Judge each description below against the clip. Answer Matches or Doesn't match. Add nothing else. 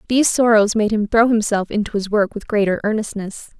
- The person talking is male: Doesn't match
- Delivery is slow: Doesn't match